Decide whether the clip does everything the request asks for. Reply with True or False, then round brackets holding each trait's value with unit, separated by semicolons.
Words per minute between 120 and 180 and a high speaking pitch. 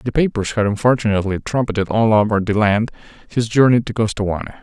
False (170 wpm; 110 Hz)